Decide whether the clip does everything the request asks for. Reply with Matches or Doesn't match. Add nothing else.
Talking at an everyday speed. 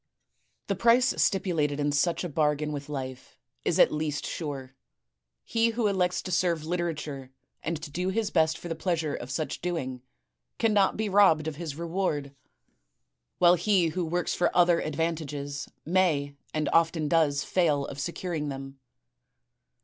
Matches